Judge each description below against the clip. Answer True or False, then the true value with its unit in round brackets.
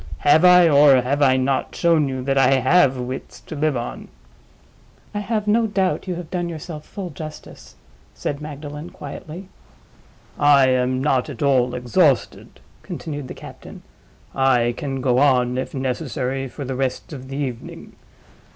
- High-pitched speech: False (140 Hz)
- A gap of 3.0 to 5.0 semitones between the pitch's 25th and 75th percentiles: True (3.4 semitones)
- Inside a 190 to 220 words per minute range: False (160 wpm)